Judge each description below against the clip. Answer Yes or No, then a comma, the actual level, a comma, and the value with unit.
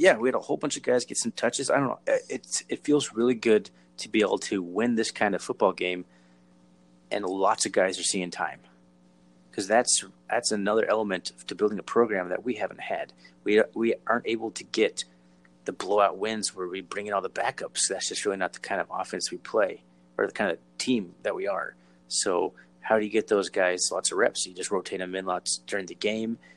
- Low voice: Yes, very low, 90 Hz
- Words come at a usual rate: No, fast, 230 wpm